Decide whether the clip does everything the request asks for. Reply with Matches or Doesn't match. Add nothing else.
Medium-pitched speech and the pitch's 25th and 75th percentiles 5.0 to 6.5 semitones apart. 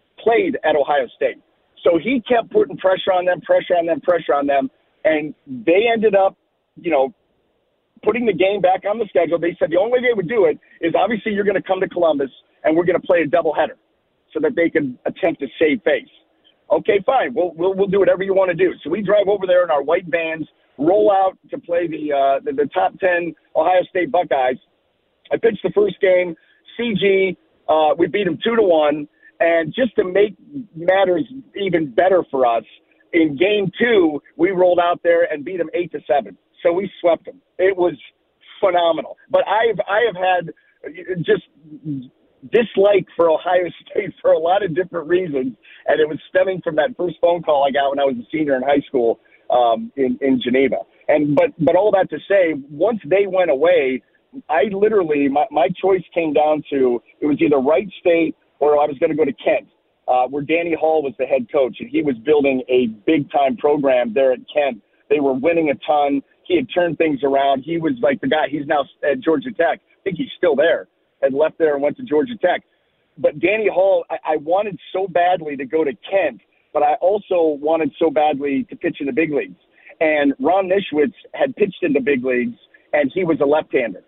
Matches